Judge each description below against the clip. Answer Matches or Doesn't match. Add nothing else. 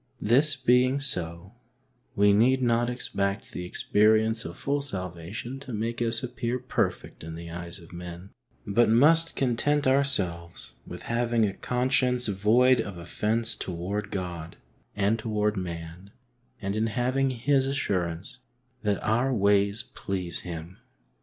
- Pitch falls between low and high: Doesn't match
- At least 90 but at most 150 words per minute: Matches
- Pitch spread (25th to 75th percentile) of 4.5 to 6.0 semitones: Matches